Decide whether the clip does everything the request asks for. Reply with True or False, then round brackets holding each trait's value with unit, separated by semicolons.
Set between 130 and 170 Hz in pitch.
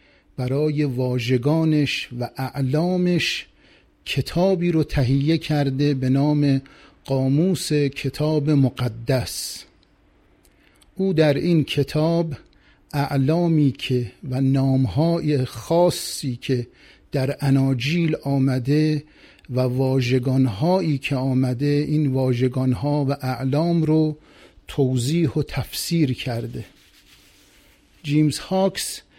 True (140 Hz)